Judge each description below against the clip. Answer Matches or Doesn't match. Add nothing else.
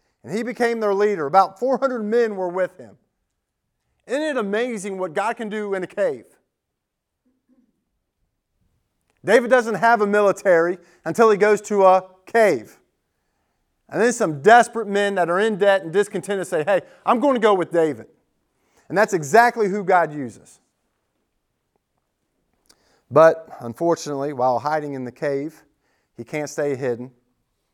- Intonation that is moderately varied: Doesn't match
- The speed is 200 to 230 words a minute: Doesn't match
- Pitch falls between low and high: Doesn't match